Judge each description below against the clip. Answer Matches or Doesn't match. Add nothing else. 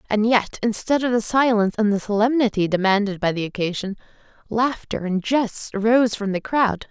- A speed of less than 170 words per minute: Doesn't match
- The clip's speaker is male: Doesn't match